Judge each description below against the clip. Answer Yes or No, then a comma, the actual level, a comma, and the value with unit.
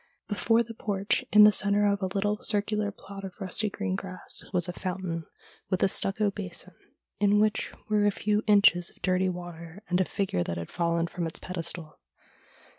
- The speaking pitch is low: No, high, 195 Hz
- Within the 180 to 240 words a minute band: Yes, average, 190 wpm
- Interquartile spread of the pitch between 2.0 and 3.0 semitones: Yes, average, 2.7 semitones